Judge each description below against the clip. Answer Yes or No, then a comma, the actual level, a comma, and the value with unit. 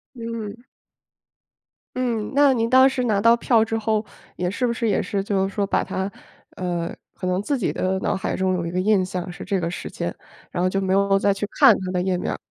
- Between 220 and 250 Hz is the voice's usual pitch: No, high, 200 Hz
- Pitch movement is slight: No, average, 3.7 semitones